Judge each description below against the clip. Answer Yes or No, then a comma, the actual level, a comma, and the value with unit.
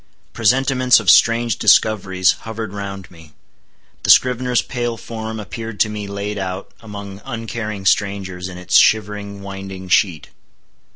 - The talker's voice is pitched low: Yes, low, 100 Hz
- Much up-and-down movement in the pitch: No, average, 2.8 semitones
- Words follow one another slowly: Yes, slow, 130 wpm